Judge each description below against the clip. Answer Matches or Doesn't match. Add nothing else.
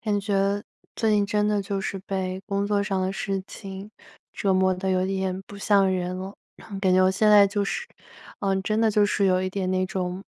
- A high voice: Matches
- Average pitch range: Doesn't match